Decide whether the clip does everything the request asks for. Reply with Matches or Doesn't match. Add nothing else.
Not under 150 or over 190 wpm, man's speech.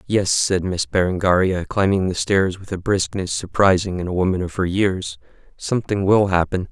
Matches